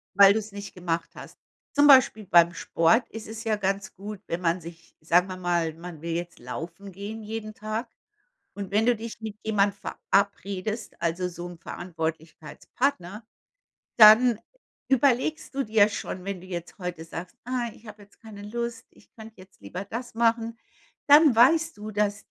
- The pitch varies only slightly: No, average, 4.2 semitones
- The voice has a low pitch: No, high, 205 Hz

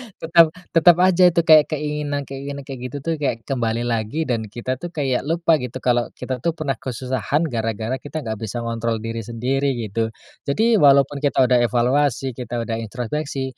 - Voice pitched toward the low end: Yes, low, 130 Hz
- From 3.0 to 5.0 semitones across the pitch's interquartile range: Yes, average, 4.2 semitones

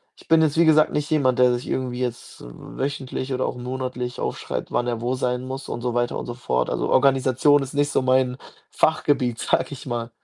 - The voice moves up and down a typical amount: No, narrow, 2.3 semitones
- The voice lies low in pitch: Yes, low, 130 Hz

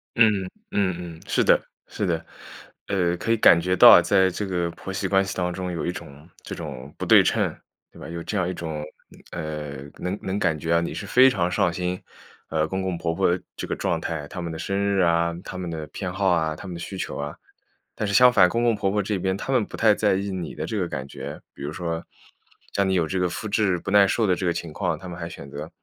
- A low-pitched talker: Yes, very low, 90 Hz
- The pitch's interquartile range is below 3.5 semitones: Yes, average, 2.9 semitones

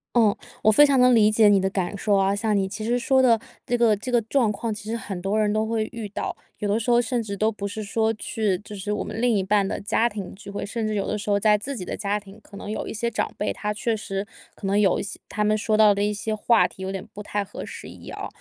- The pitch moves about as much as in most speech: No, narrow, 1.8 semitones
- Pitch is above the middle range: Yes, high, 210 Hz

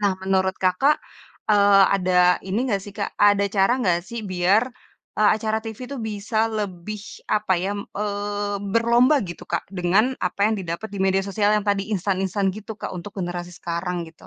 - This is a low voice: No, high, 200 Hz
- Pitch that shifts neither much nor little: No, narrow, 2.2 semitones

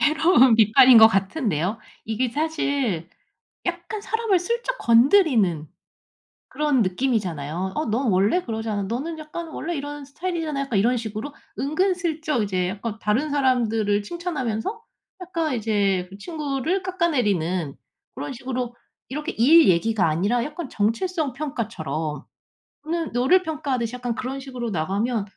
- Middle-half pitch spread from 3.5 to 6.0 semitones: No, wide, 6.8 semitones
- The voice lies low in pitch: No, very high, 250 Hz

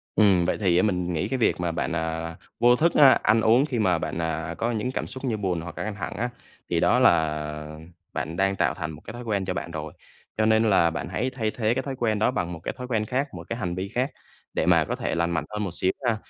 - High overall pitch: No, low, 100 Hz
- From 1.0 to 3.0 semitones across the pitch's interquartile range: No, wide, 5.5 semitones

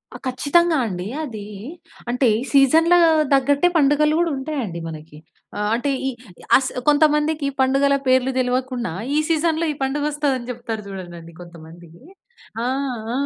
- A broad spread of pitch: Yes, wide, 5.9 semitones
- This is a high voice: Yes, very high, 265 Hz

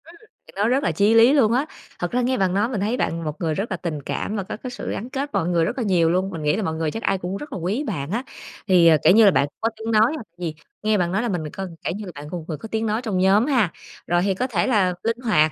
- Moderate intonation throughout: Yes, average, 4.8 semitones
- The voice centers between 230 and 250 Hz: No, high, 200 Hz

